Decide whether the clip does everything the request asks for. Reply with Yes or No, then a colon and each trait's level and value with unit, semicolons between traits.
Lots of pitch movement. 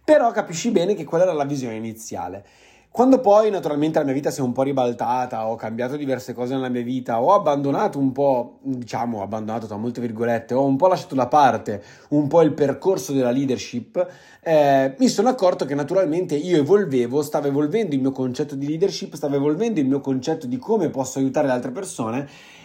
Yes: wide, 6.0 semitones